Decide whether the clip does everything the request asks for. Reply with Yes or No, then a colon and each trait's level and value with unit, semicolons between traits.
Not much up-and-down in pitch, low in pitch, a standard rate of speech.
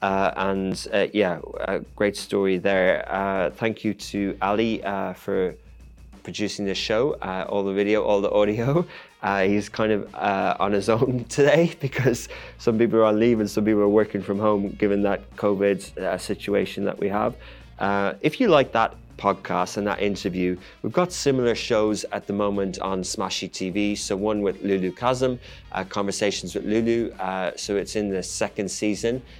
Yes: narrow, 2.2 semitones; low, 100 Hz; average, 180 wpm